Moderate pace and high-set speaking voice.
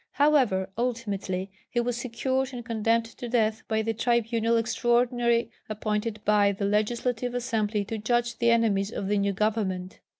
Yes: average, 155 wpm; high, 225 Hz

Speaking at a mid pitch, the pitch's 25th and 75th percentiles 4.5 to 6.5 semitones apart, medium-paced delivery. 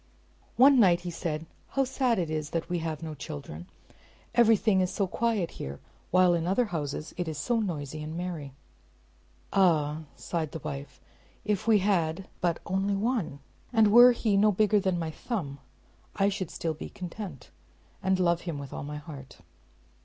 Yes: medium, 175 Hz; average, 4.9 semitones; average, 175 wpm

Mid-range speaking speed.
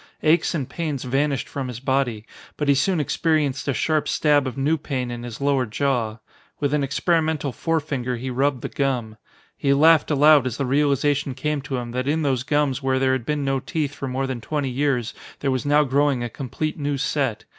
No: fast, 210 wpm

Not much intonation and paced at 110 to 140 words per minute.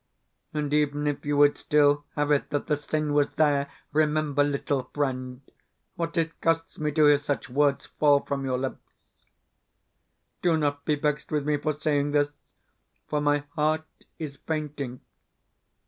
No: narrow, 1.0 semitones; average, 160 wpm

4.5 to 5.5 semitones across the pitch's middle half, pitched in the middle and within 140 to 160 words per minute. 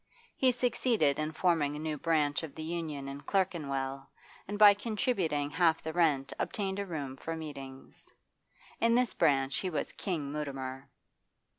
Yes: average, 5.2 semitones; medium, 155 Hz; average, 155 wpm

